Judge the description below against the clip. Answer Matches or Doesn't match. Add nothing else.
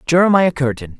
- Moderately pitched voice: Matches